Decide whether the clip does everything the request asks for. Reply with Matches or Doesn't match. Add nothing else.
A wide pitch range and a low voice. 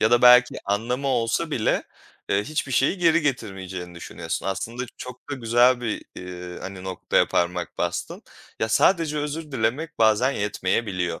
Matches